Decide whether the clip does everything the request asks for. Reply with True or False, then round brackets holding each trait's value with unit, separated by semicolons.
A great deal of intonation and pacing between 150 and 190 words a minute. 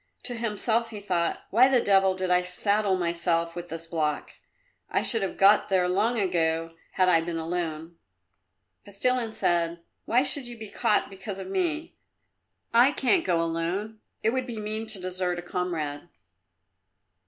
False (4.5 semitones; 165 wpm)